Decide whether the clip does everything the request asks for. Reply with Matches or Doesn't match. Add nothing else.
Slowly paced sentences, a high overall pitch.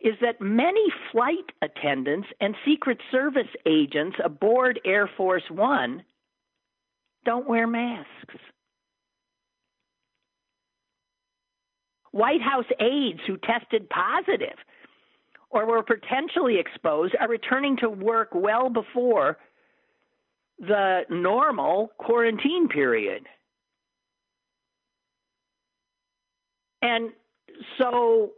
Matches